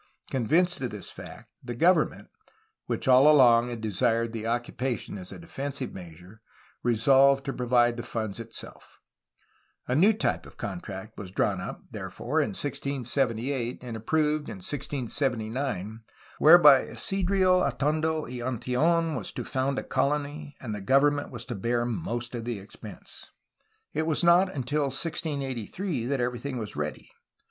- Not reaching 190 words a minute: Yes, average, 150 wpm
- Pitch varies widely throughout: No, average, 4.1 semitones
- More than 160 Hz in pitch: No, low, 130 Hz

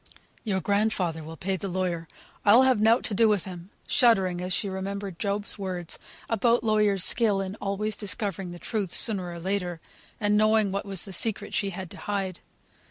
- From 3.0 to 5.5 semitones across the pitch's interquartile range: No, narrow, 2.5 semitones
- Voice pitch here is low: No, high, 195 Hz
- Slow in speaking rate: No, average, 185 wpm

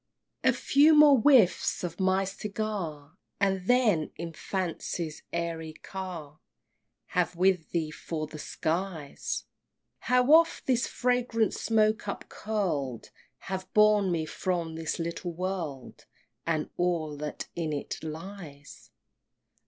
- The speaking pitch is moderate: Yes, medium, 180 Hz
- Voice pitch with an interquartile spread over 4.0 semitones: Yes, average, 4.7 semitones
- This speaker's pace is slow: Yes, slow, 120 wpm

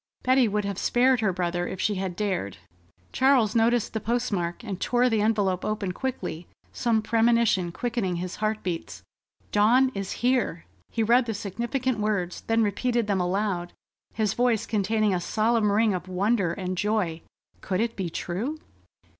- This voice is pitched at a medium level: No, high, 210 Hz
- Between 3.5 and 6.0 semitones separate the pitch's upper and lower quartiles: Yes, average, 4.1 semitones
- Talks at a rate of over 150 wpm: Yes, average, 165 wpm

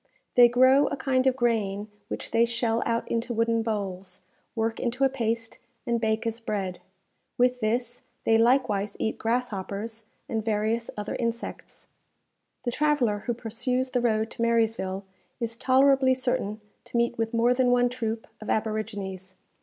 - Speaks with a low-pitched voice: No, high, 230 Hz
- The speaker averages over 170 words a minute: No, average, 155 wpm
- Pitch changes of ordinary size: No, narrow, 2.2 semitones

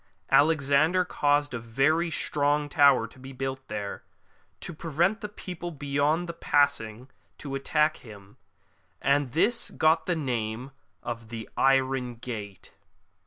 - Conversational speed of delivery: No, slow, 130 wpm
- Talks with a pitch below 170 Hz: Yes, medium, 140 Hz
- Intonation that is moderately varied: Yes, average, 4.3 semitones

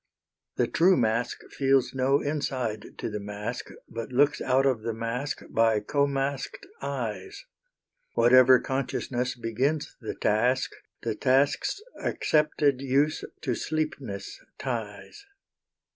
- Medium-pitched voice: No, low, 130 Hz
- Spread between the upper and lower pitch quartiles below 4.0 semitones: Yes, average, 3.6 semitones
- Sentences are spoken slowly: Yes, slow, 115 wpm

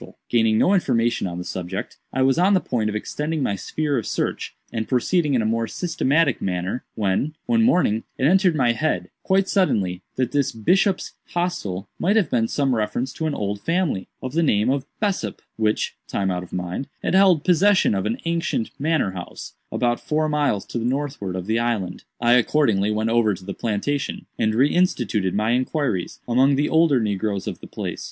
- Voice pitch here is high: No, low, 125 Hz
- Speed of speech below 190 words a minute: No, average, 195 wpm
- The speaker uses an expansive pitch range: Yes, wide, 6.8 semitones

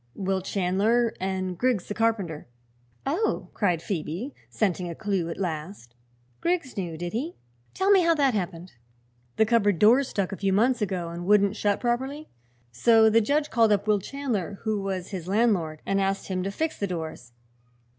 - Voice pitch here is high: Yes, high, 200 Hz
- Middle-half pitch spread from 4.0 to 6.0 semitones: Yes, average, 4.5 semitones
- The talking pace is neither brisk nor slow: Yes, average, 175 wpm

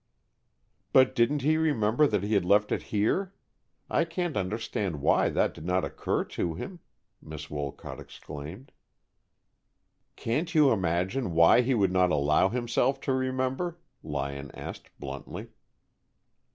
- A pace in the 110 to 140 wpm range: Yes, slow, 135 wpm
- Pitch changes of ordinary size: No, wide, 8.1 semitones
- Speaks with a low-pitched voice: Yes, low, 105 Hz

